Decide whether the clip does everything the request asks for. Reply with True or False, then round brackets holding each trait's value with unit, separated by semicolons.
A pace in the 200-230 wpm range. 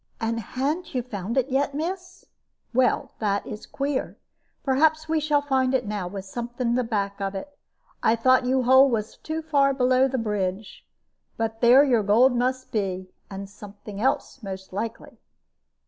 False (170 wpm)